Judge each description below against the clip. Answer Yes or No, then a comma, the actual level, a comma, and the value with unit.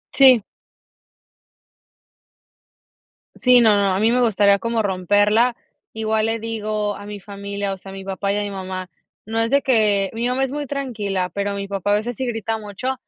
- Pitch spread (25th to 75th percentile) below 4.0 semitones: Yes, average, 2.7 semitones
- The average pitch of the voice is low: No, high, 210 Hz